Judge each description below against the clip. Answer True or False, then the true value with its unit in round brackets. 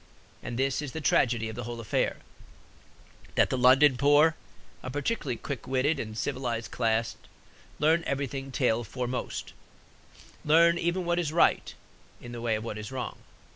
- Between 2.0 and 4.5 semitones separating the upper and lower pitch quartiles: True (4.0 semitones)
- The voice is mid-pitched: False (130 Hz)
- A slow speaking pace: False (160 wpm)